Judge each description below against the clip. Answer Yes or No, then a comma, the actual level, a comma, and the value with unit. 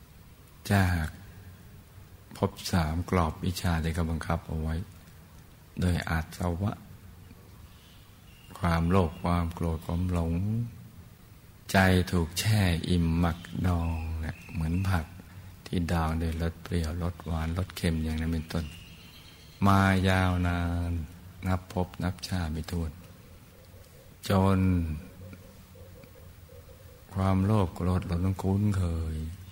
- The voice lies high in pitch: No, very low, 90 Hz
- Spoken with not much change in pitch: Yes, narrow, 2.2 semitones